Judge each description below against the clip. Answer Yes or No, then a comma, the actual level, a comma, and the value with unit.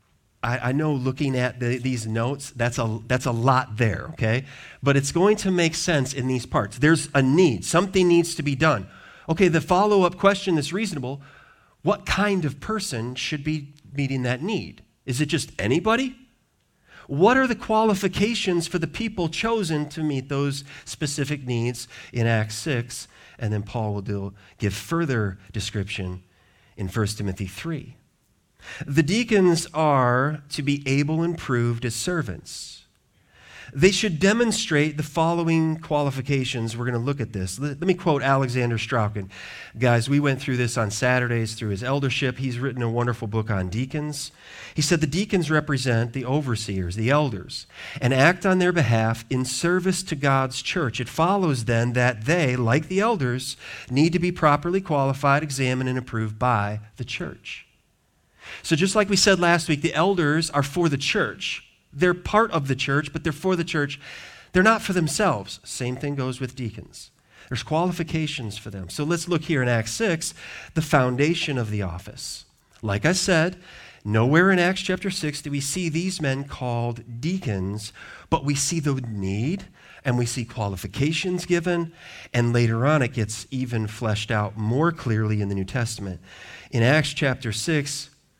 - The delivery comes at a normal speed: Yes, average, 170 wpm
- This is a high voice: No, medium, 140 Hz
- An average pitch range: No, wide, 5.7 semitones